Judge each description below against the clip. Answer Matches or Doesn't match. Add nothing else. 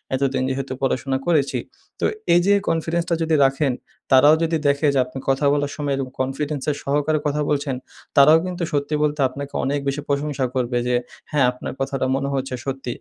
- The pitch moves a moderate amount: Doesn't match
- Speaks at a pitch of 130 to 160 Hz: Matches